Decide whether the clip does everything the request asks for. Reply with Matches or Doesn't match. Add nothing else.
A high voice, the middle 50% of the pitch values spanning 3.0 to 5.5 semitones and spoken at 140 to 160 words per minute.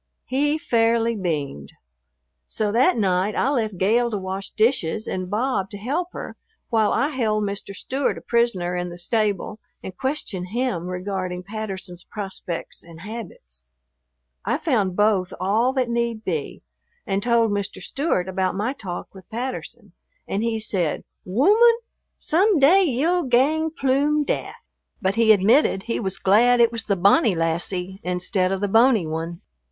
Matches